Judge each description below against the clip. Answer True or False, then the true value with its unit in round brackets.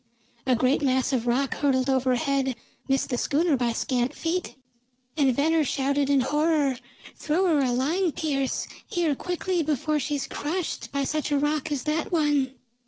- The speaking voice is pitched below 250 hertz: False (280 Hz)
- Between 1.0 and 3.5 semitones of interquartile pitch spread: True (2.8 semitones)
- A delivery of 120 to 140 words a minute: False (170 wpm)